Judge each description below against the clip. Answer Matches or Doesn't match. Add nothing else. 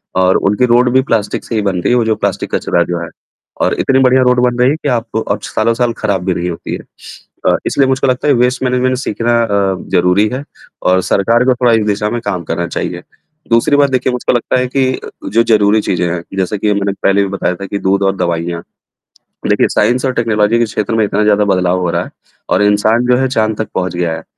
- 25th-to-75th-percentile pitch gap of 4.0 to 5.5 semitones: Matches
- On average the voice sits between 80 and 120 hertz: Matches